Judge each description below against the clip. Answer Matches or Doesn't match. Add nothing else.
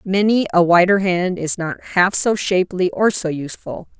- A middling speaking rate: Matches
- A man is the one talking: Doesn't match